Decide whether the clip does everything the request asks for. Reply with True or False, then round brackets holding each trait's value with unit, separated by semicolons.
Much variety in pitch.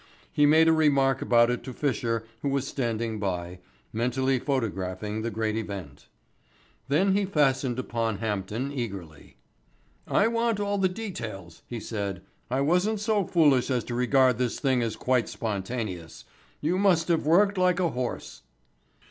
True (6.5 semitones)